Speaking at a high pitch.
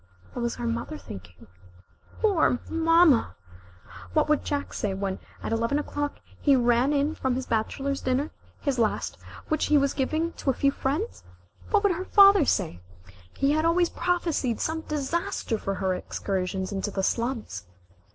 Yes: very high, 275 Hz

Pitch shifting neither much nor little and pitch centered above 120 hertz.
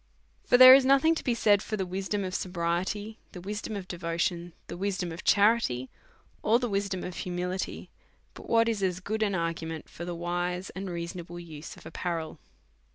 Yes: average, 3.4 semitones; medium, 185 Hz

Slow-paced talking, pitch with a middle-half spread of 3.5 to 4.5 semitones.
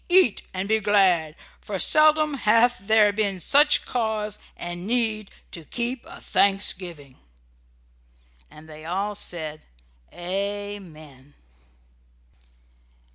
Yes: slow, 100 wpm; average, 4.1 semitones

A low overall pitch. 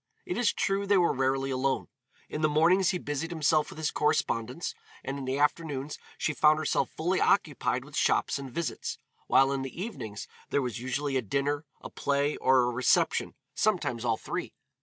No: medium, 145 Hz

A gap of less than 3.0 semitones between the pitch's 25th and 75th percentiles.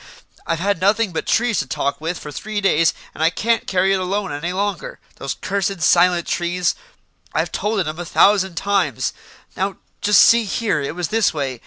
No: average, 3.6 semitones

